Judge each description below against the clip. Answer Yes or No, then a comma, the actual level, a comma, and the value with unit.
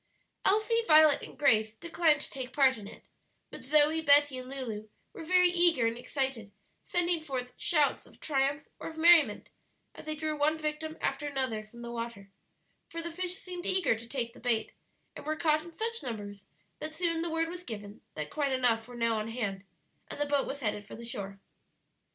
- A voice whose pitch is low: No, very high, 280 Hz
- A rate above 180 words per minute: Yes, average, 200 wpm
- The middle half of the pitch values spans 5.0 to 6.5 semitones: Yes, wide, 5.6 semitones